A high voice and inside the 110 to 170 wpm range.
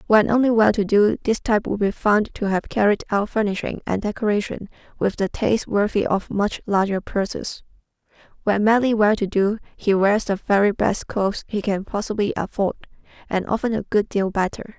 No: high, 205 Hz; average, 185 wpm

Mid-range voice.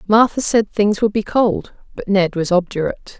No: high, 200 Hz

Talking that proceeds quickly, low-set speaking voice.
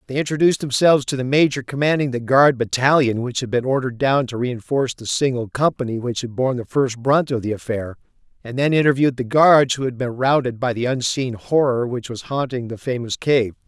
Yes: fast, 210 wpm; low, 130 Hz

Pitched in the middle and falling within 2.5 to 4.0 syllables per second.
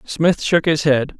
Yes: medium, 155 Hz; 3.7 syllables/s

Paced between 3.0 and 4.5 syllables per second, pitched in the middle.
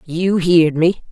Yes: 3.1 syllables/s; medium, 170 Hz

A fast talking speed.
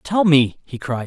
Yes: fast, 225 wpm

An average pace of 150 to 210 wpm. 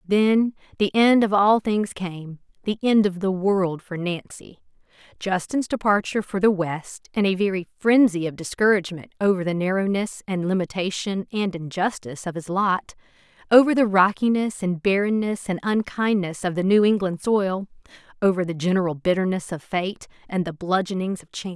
Yes: average, 160 wpm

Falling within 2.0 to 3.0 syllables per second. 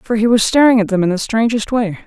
No: 6.1 syllables/s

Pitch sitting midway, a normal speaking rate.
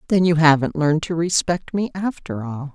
Yes: medium, 160 Hz; average, 195 wpm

